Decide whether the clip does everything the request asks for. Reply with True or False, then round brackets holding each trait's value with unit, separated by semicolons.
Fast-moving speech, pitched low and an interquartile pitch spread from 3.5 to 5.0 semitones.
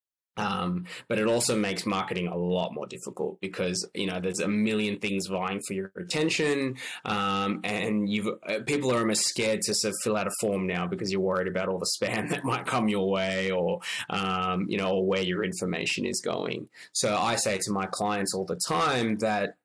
False (210 wpm; 100 Hz; 2.5 semitones)